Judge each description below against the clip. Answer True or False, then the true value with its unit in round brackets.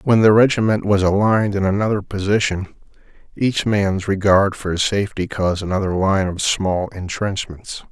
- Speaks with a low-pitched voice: True (100 Hz)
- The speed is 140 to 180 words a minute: True (150 wpm)